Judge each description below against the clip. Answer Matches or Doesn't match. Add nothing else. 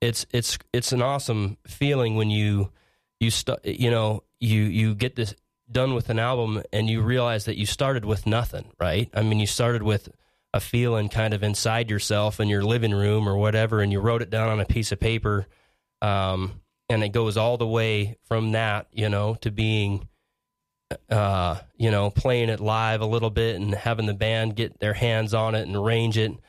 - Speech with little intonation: Matches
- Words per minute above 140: Matches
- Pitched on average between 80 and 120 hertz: Matches